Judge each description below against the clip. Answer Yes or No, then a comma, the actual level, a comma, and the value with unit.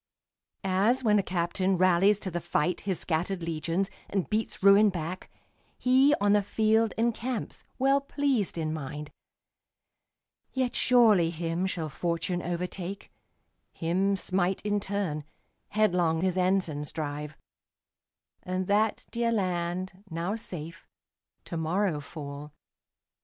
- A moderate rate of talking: No, slow, 120 wpm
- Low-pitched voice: No, medium, 185 Hz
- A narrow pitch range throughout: No, average, 3.7 semitones